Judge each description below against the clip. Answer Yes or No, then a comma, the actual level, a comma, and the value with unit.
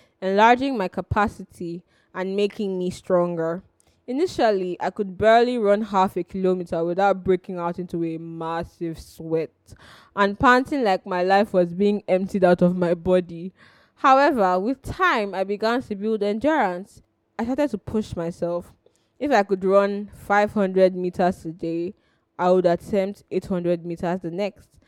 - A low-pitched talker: No, high, 190 Hz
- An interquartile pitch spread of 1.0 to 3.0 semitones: Yes, narrow, 2.6 semitones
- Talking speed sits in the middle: Yes, average, 150 wpm